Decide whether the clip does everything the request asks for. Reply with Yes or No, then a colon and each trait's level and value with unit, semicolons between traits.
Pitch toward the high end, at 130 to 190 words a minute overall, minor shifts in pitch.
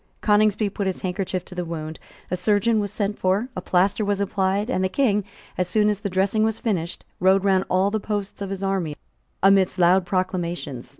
No: high, 195 Hz; average, 200 wpm; narrow, 2.1 semitones